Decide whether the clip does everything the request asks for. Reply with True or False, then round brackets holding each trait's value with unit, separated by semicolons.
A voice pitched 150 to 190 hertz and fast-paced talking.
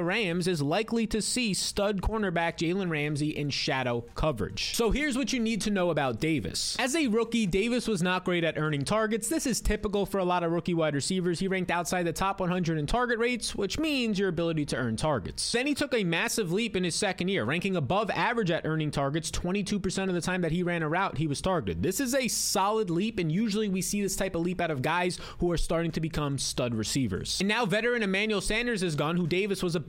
True (185 Hz; 240 wpm)